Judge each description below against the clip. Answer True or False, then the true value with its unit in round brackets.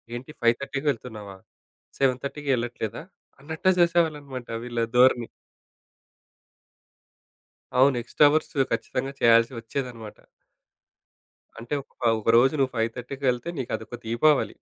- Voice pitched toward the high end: False (125 Hz)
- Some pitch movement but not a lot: True (3.1 semitones)